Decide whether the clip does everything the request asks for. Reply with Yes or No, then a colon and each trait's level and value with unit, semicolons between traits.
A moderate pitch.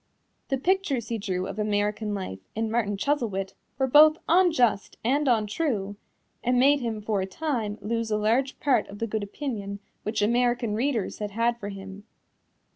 No: high, 225 Hz